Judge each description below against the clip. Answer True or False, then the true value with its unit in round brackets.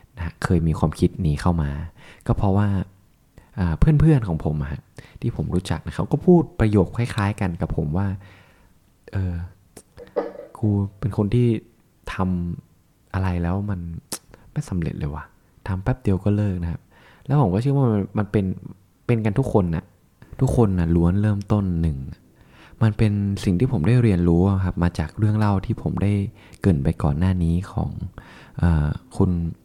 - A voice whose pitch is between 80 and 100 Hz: True (95 Hz)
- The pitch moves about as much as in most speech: True (3.9 semitones)